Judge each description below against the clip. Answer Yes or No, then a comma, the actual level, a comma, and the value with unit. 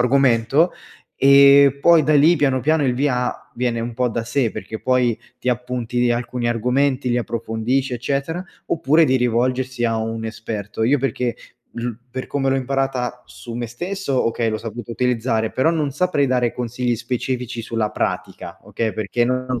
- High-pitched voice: No, low, 125 Hz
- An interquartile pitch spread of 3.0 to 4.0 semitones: No, narrow, 2.6 semitones